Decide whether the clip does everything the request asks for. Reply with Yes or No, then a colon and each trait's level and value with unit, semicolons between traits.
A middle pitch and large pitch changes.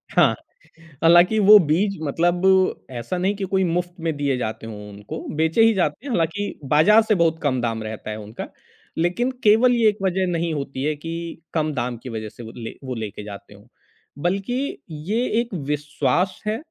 Yes: medium, 165 Hz; wide, 7.2 semitones